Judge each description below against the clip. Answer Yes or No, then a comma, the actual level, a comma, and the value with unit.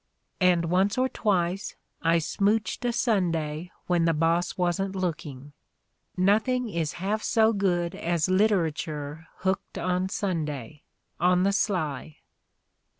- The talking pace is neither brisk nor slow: No, slow, 125 wpm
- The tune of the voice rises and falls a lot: No, average, 3.3 semitones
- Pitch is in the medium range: Yes, medium, 180 Hz